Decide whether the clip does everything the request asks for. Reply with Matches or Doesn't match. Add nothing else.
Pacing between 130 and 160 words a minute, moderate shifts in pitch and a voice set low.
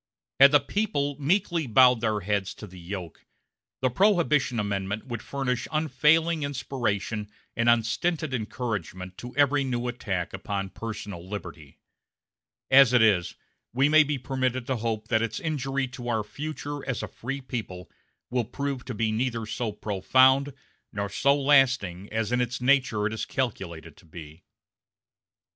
Matches